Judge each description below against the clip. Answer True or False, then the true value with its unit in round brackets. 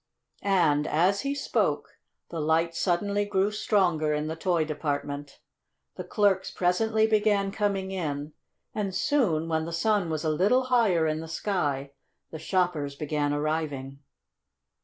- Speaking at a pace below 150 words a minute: True (140 wpm)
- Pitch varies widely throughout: False (4.7 semitones)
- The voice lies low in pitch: False (170 Hz)